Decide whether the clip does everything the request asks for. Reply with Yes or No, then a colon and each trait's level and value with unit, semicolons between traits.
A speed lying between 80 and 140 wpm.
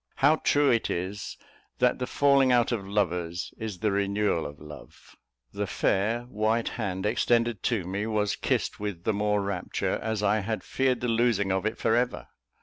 No: average, 180 wpm